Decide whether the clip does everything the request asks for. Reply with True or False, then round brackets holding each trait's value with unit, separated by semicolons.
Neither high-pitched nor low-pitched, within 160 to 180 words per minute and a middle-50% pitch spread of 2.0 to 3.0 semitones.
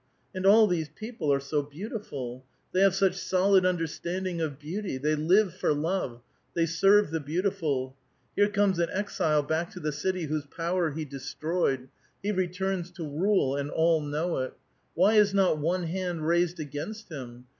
False (170 Hz; 175 wpm; 4.2 semitones)